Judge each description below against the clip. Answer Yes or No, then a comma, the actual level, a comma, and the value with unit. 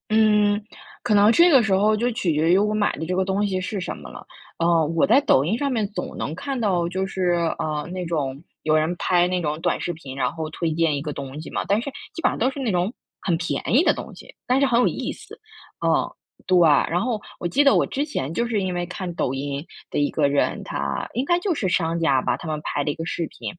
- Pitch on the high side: No, medium, 180 Hz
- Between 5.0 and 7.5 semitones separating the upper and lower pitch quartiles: Yes, wide, 5.4 semitones